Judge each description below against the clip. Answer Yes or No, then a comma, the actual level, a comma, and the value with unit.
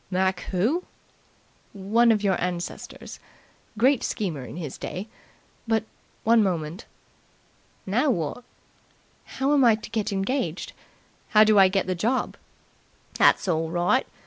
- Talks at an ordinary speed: No, slow, 130 wpm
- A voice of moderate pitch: No, high, 200 Hz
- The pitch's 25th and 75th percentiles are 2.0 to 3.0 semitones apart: No, average, 4.4 semitones